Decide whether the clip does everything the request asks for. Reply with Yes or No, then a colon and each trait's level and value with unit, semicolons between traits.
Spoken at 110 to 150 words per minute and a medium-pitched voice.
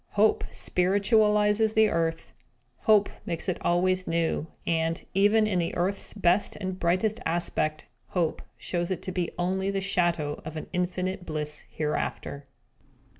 Yes: average, 140 wpm; medium, 180 Hz